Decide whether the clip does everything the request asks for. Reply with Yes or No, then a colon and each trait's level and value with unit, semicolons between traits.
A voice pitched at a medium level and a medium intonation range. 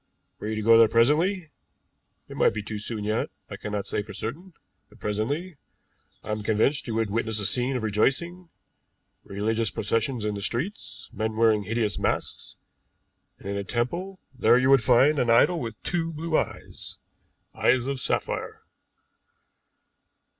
No: low, 115 Hz; average, 4.7 semitones